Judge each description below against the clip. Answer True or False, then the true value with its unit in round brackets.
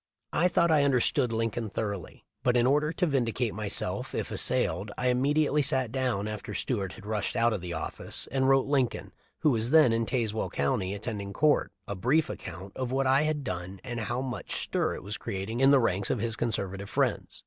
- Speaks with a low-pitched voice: True (120 Hz)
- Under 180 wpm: False (205 wpm)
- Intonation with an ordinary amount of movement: True (4.6 semitones)